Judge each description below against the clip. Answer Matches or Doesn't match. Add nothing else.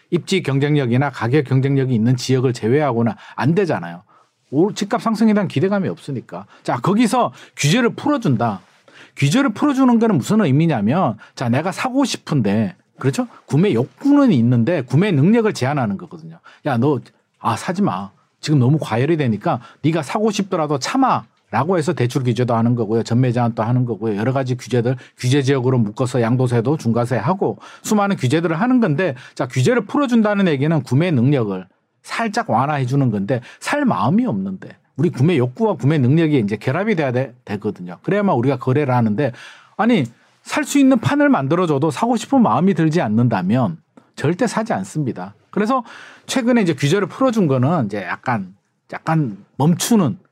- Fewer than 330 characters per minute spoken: Doesn't match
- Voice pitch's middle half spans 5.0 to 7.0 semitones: Doesn't match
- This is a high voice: Doesn't match